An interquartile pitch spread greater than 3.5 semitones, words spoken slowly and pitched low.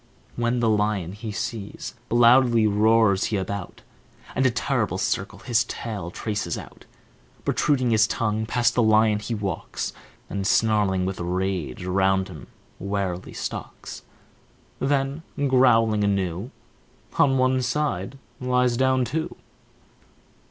Yes: average, 4.1 semitones; slow, 125 wpm; low, 110 Hz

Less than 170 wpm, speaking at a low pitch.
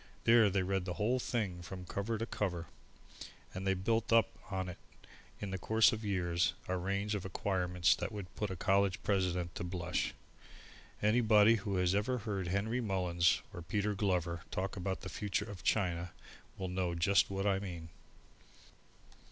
No: average, 175 wpm; very low, 95 Hz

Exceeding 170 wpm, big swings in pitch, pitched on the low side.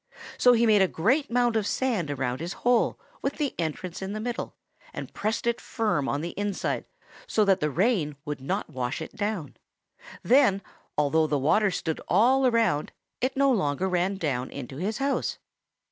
No: average, 185 wpm; wide, 7.5 semitones; high, 195 Hz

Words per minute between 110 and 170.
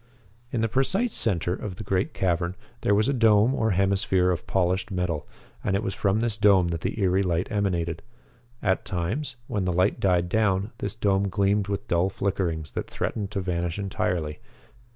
No: average, 185 wpm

